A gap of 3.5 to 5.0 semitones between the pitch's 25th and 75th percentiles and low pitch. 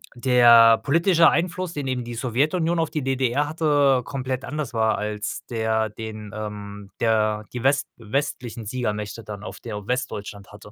Yes: average, 4.5 semitones; low, 120 Hz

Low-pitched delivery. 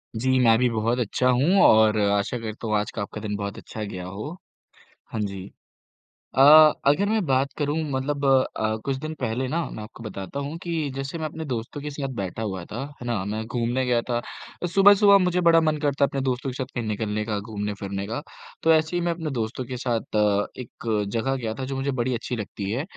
Yes: low, 125 Hz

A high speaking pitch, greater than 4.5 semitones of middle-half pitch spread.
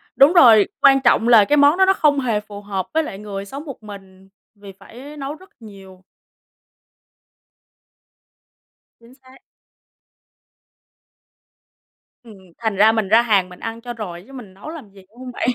Yes: high, 225 Hz; average, 5.2 semitones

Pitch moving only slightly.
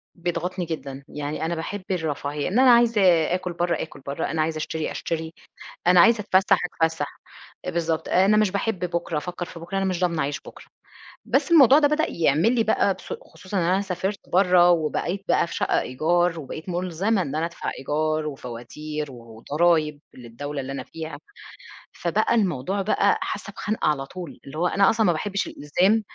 No: average, 4.0 semitones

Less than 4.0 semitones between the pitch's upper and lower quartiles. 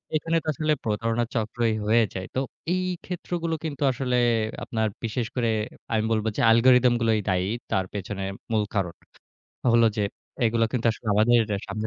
Yes: average, 2.7 semitones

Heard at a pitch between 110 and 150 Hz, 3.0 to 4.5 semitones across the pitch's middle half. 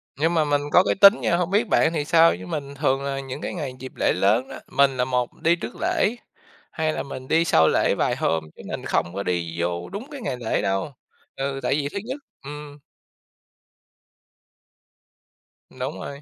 No: medium, 140 Hz; average, 4.9 semitones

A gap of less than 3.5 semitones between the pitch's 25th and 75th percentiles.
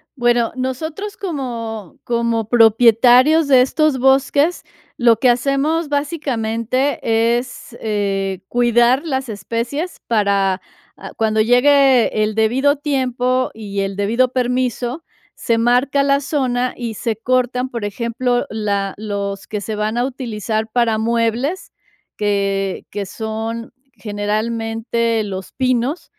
Yes: average, 3.1 semitones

